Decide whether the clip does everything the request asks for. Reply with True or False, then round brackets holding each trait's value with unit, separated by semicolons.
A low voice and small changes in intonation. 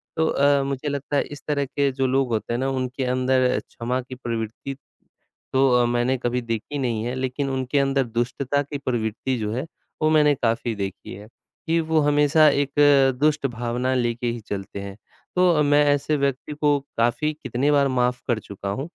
False (130 Hz; 3.0 semitones)